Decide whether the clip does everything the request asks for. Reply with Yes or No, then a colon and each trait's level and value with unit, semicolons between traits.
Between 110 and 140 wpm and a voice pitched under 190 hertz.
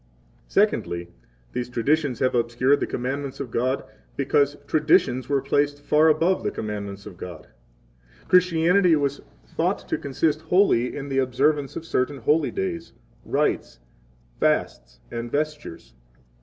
Yes: slow, 135 wpm; medium, 140 Hz